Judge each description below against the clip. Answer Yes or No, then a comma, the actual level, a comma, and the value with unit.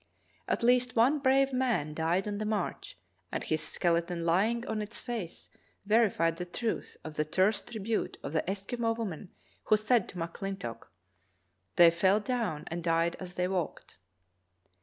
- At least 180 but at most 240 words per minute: No, average, 160 wpm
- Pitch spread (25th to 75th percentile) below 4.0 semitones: No, average, 5.3 semitones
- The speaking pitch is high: Yes, high, 195 Hz